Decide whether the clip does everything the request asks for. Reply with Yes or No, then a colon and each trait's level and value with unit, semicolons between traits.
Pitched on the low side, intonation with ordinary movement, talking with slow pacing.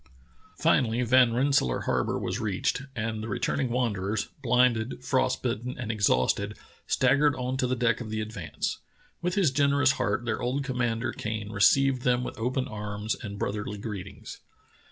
No: low, 115 Hz; average, 3.1 semitones; average, 160 wpm